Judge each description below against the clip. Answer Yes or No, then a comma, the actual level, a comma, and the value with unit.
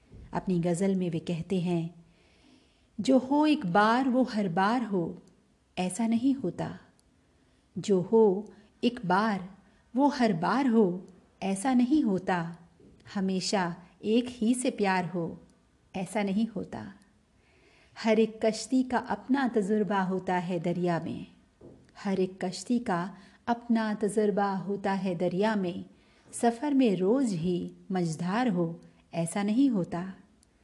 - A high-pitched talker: Yes, high, 200 Hz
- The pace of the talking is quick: No, average, 130 wpm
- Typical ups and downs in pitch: Yes, average, 4.0 semitones